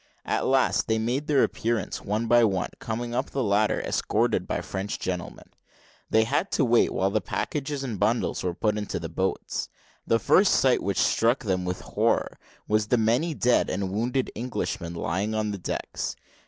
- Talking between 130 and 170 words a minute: No, average, 180 wpm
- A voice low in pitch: Yes, low, 110 Hz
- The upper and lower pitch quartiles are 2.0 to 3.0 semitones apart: No, average, 3.8 semitones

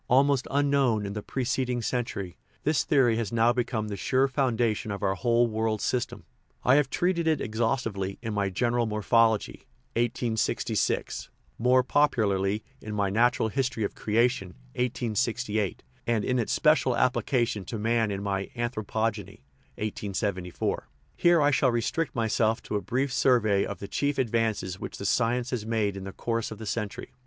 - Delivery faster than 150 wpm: Yes, average, 165 wpm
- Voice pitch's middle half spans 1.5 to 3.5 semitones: Yes, average, 3.1 semitones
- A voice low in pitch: Yes, low, 115 Hz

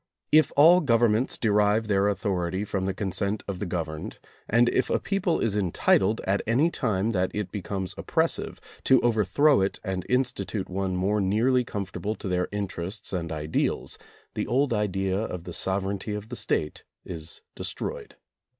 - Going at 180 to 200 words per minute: No, average, 170 wpm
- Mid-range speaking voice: No, low, 100 Hz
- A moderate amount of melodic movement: Yes, average, 3.5 semitones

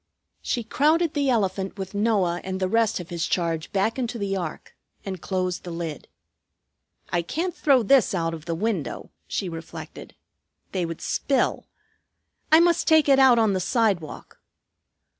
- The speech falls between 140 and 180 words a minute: Yes, average, 160 wpm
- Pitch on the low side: No, high, 195 Hz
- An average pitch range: No, wide, 6.0 semitones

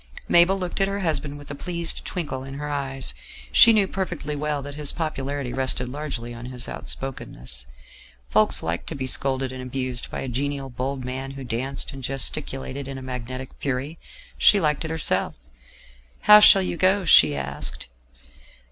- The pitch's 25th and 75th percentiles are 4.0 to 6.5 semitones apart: No, average, 3.1 semitones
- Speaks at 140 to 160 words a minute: No, average, 175 wpm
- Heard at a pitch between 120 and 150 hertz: Yes, low, 135 Hz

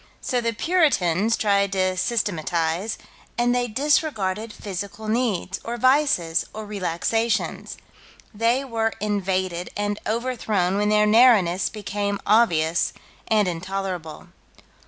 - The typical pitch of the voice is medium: No, high, 205 Hz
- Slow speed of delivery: Yes, slow, 110 wpm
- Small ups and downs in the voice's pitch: No, average, 3.7 semitones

